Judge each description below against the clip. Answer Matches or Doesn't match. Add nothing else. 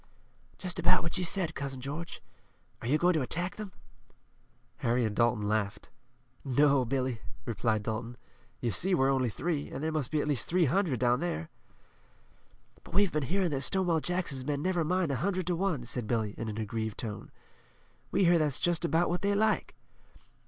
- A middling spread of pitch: Doesn't match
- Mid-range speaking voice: Matches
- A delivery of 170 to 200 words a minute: Matches